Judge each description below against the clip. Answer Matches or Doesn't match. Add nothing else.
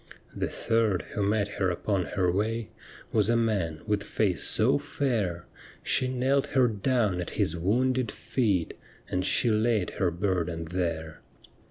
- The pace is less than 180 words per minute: Matches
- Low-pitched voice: Matches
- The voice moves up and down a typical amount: Matches